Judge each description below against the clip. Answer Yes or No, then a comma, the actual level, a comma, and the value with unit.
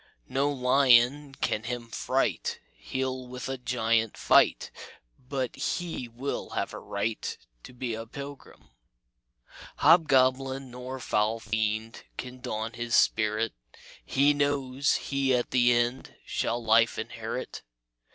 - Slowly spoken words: Yes, slow, 120 wpm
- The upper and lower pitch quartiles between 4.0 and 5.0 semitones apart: No, average, 2.7 semitones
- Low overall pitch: Yes, low, 125 Hz